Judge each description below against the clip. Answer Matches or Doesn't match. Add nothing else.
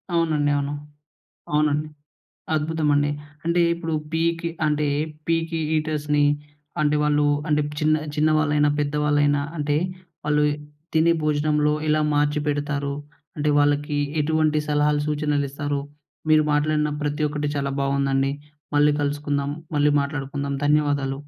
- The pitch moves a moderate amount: Doesn't match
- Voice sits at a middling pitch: Matches